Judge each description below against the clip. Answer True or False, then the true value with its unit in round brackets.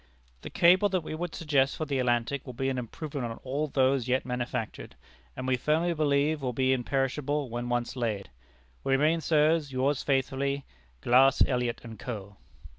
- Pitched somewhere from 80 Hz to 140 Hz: True (135 Hz)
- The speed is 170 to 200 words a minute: True (175 wpm)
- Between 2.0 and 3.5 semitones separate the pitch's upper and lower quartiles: True (3.1 semitones)